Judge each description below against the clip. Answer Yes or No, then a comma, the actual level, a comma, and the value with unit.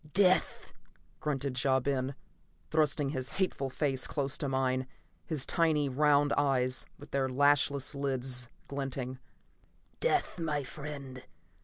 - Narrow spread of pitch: Yes, narrow, 1.9 semitones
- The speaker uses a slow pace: Yes, slow, 120 wpm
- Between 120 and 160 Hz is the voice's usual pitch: Yes, medium, 140 Hz